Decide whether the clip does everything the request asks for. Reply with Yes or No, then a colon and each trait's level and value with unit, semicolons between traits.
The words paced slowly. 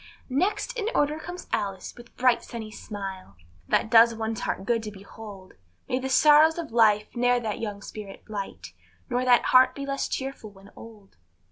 No: average, 175 wpm